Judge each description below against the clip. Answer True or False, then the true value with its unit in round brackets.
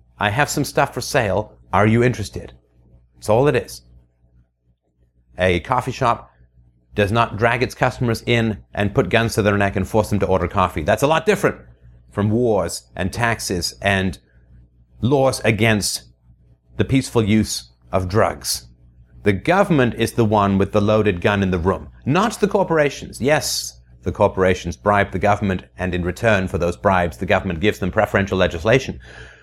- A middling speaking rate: True (170 wpm)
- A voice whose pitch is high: False (95 Hz)